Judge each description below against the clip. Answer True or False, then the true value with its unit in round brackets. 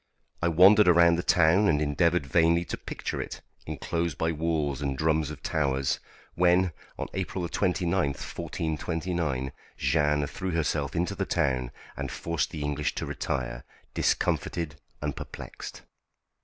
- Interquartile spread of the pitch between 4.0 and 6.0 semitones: False (2.9 semitones)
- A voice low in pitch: True (80 Hz)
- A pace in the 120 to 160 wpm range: True (140 wpm)